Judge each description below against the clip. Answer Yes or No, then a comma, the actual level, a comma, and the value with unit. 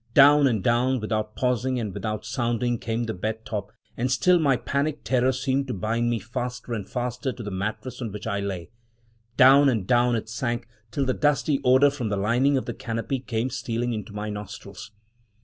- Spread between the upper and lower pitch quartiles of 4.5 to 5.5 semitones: No, average, 3.1 semitones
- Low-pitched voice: Yes, low, 120 Hz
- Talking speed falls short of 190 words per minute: No, average, 200 wpm